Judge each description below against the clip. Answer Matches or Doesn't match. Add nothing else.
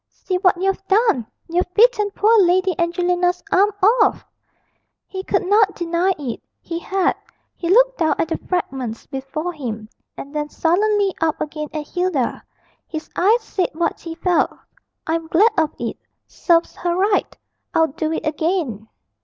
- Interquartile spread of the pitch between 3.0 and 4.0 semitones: Matches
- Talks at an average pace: Matches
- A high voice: Matches